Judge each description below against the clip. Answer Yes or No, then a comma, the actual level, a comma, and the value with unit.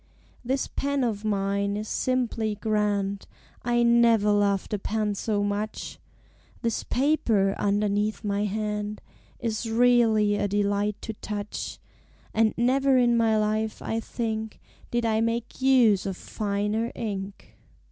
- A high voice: Yes, high, 215 Hz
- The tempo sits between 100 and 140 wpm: Yes, slow, 135 wpm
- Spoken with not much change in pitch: Yes, narrow, 2.2 semitones